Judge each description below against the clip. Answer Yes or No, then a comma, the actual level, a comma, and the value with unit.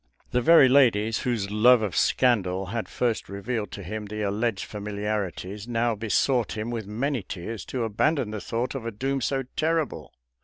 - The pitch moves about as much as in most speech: Yes, average, 3.1 semitones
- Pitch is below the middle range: Yes, low, 110 Hz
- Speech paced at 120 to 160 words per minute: No, average, 175 wpm